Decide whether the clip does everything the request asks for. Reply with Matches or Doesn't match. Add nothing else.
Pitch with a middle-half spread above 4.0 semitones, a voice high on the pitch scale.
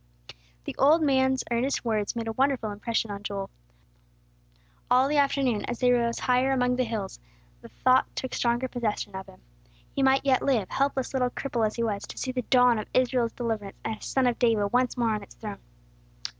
Doesn't match